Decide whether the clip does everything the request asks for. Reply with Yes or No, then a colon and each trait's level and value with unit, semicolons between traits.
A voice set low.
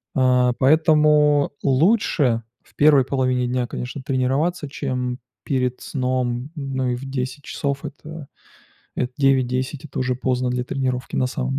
Yes: low, 130 Hz